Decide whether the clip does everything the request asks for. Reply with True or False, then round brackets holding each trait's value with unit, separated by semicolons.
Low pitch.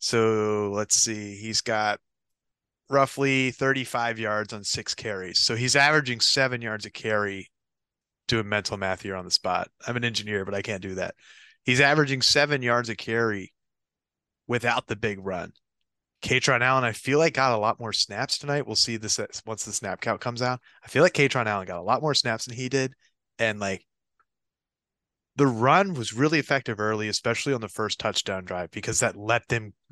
True (115 Hz)